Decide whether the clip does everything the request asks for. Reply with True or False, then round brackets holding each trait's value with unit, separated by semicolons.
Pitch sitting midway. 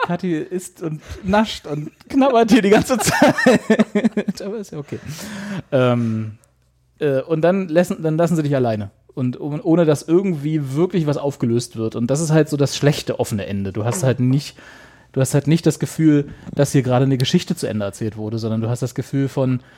True (145 Hz)